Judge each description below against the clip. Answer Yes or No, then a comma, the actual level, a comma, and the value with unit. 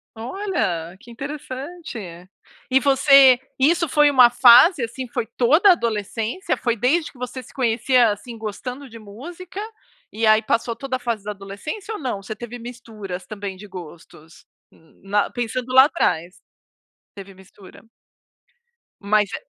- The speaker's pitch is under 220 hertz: No, high, 240 Hz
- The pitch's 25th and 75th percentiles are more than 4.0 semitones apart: Yes, average, 4.5 semitones